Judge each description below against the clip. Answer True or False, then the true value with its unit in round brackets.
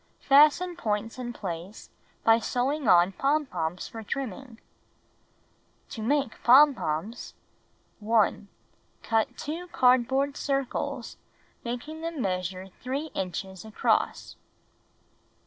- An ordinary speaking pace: False (95 wpm)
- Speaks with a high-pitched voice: True (240 Hz)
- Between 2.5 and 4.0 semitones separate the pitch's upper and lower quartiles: False (5.6 semitones)